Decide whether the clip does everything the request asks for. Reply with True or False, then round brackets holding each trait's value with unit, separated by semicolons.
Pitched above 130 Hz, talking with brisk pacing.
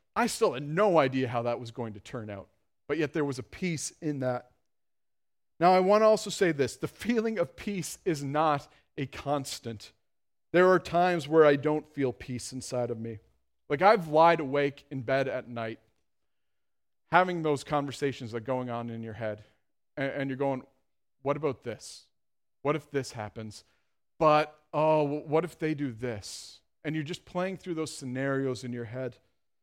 False (140 Hz; 185 wpm)